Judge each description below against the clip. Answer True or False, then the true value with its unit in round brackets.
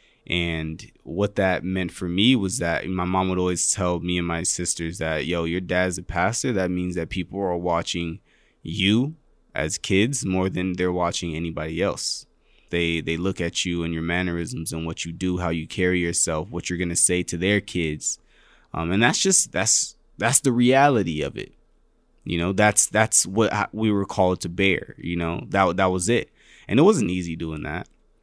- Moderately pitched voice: False (90 Hz)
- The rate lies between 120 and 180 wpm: False (200 wpm)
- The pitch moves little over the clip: True (2.3 semitones)